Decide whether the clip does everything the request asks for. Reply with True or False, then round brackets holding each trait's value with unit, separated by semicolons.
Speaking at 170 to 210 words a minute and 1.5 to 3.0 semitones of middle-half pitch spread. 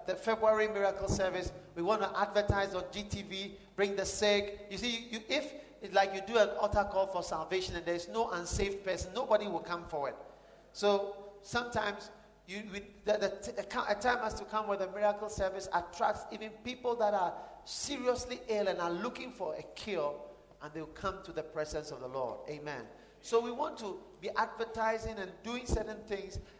True (190 wpm; 2.7 semitones)